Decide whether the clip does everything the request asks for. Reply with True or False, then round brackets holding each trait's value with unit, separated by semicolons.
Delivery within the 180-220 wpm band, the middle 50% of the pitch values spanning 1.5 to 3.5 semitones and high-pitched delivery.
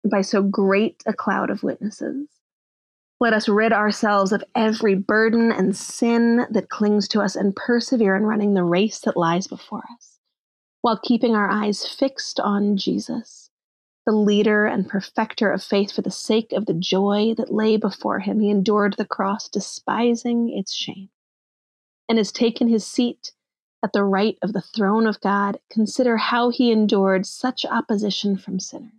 False (170 wpm; 2.6 semitones; 210 Hz)